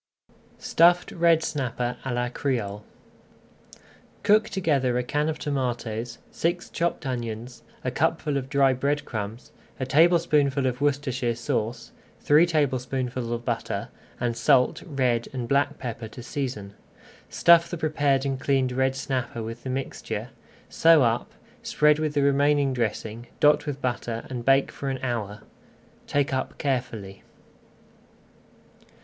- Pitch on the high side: No, low, 130 Hz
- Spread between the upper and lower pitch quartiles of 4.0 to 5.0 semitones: No, average, 3.4 semitones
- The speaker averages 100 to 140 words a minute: Yes, slow, 135 wpm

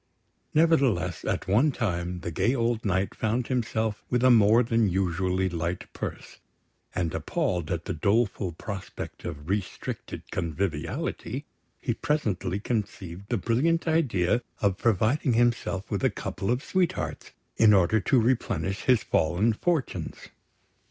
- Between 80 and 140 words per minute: Yes, slow, 135 wpm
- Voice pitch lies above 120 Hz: No, low, 105 Hz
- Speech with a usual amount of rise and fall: Yes, average, 4.9 semitones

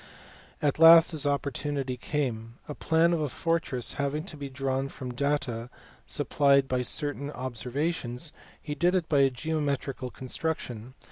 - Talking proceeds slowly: No, average, 155 wpm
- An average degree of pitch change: Yes, average, 3.1 semitones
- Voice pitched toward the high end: No, medium, 140 Hz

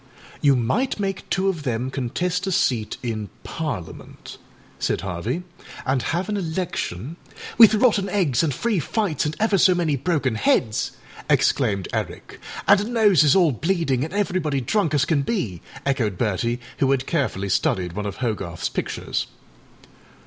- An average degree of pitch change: No, wide, 8.1 semitones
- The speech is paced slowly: No, average, 150 wpm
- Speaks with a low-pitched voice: No, medium, 145 Hz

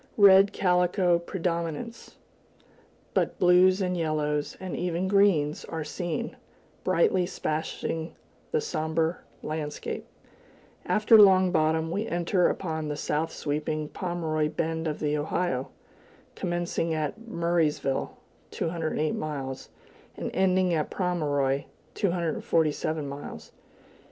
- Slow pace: Yes, slow, 105 wpm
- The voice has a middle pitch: Yes, medium, 165 Hz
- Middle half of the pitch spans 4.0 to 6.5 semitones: No, average, 2.9 semitones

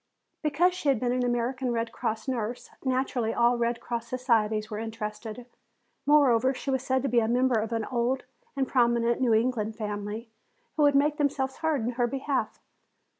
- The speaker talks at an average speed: Yes, average, 180 wpm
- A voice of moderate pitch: No, high, 245 Hz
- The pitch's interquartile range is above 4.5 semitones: No, average, 2.7 semitones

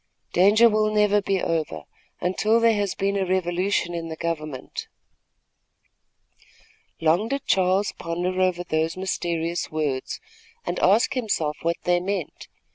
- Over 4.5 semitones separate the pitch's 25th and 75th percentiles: No, average, 3.2 semitones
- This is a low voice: No, medium, 180 Hz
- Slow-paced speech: Yes, slow, 130 wpm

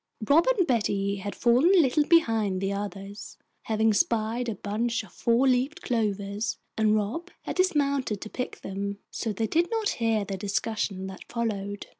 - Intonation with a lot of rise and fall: No, average, 4.1 semitones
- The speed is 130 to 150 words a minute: No, average, 170 wpm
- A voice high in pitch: Yes, high, 220 Hz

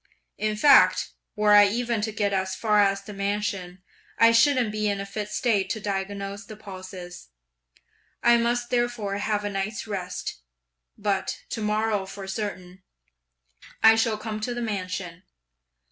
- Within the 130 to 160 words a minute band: Yes, average, 155 wpm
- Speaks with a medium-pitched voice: No, high, 205 Hz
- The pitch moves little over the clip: Yes, narrow, 2.1 semitones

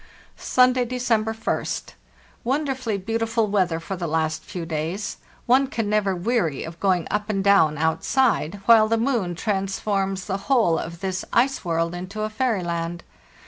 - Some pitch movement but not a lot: Yes, average, 4.8 semitones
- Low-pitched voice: No, high, 200 Hz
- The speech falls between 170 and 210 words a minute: No, average, 160 wpm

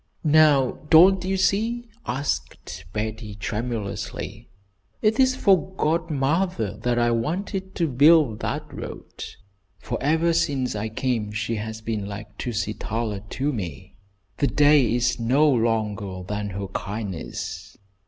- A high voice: No, low, 120 Hz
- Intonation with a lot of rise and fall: Yes, wide, 6.9 semitones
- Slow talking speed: Yes, slow, 125 wpm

